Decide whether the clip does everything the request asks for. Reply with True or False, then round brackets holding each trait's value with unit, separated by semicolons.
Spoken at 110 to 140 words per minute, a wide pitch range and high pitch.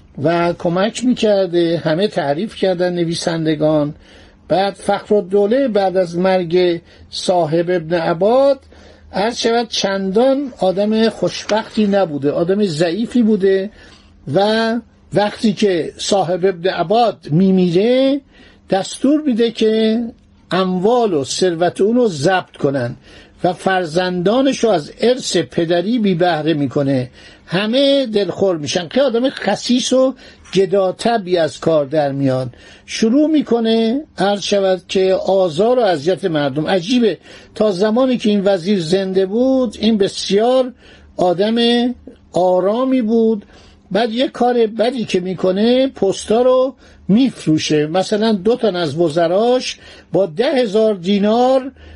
False (120 wpm; 4.6 semitones; 195 Hz)